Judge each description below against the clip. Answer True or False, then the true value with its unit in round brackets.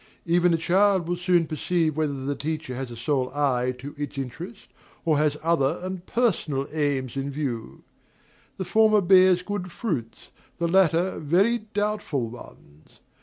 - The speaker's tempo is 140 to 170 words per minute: True (155 wpm)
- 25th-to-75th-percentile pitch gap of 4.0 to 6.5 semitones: True (5.1 semitones)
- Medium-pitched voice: True (160 Hz)